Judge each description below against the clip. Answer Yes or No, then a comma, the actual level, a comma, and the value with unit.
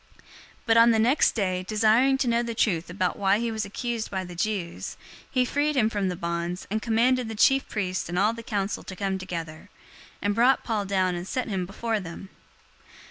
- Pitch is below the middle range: No, high, 210 Hz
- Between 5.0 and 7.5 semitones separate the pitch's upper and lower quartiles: No, average, 3.9 semitones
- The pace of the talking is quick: Yes, fast, 210 wpm